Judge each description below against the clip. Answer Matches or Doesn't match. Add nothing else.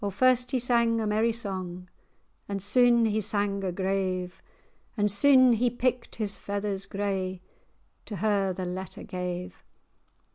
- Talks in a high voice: Matches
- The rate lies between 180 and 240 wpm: Doesn't match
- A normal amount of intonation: Matches